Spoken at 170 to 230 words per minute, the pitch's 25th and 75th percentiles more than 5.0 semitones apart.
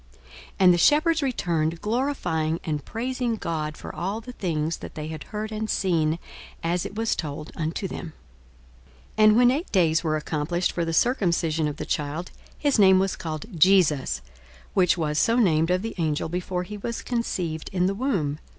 Yes: average, 185 wpm; wide, 5.4 semitones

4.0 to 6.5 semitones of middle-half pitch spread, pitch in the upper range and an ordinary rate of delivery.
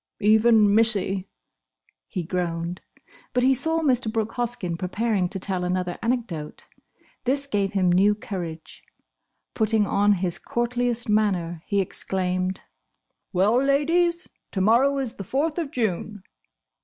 No: average, 4.9 semitones; high, 210 Hz; slow, 130 wpm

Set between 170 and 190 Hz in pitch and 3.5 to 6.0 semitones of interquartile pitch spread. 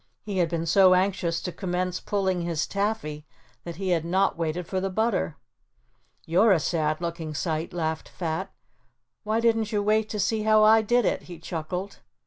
Yes: medium, 185 Hz; average, 3.8 semitones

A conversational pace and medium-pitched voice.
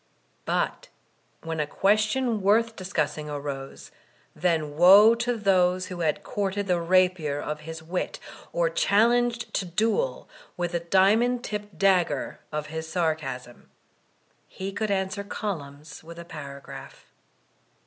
No: slow, 130 wpm; medium, 180 Hz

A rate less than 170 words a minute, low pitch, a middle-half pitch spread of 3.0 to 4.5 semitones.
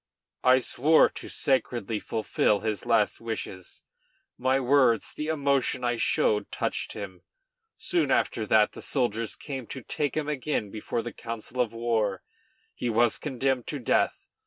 Yes: average, 150 wpm; low, 120 Hz; average, 3.4 semitones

